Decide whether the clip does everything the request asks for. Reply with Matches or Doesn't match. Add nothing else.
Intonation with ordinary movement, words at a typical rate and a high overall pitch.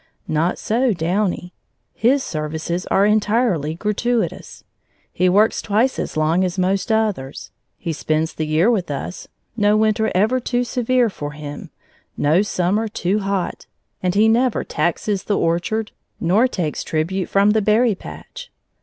Matches